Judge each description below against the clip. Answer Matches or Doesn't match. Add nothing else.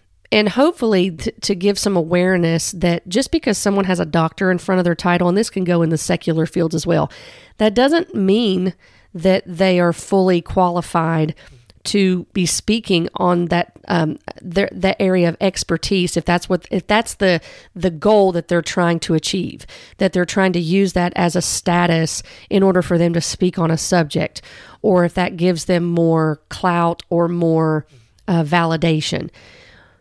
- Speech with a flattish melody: Matches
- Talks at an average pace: Matches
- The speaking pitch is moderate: Matches